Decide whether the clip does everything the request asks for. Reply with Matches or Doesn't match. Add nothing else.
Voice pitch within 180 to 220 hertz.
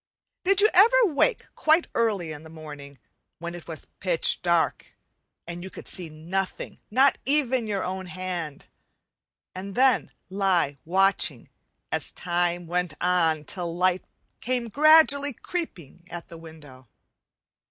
Matches